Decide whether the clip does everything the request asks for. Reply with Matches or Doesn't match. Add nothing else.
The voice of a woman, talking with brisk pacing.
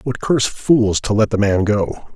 Doesn't match